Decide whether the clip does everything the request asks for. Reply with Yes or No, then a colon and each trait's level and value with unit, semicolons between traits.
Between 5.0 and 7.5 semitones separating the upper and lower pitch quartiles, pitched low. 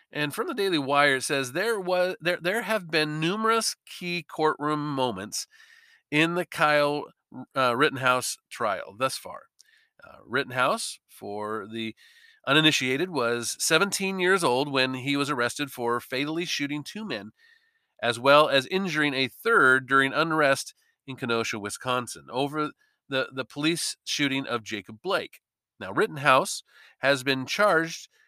No: wide, 5.4 semitones; medium, 145 Hz